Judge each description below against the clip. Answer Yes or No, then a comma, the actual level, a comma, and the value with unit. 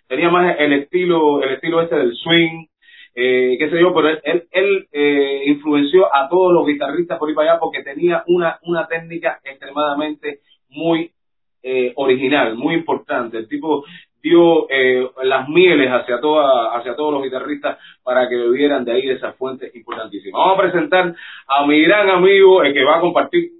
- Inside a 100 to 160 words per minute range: No, average, 185 wpm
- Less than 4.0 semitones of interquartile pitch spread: No, average, 4.3 semitones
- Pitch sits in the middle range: Yes, medium, 160 Hz